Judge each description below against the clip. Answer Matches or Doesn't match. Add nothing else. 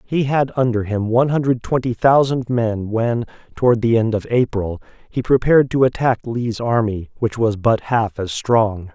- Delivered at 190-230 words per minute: Doesn't match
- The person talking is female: Doesn't match